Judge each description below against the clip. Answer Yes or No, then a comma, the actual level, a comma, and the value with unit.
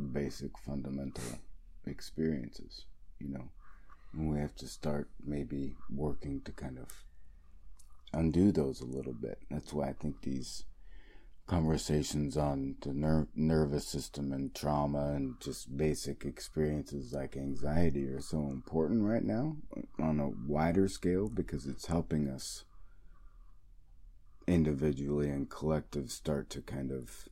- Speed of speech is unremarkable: No, slow, 130 wpm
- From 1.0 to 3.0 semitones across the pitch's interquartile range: Yes, narrow, 2.6 semitones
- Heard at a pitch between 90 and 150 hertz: No, very low, 75 Hz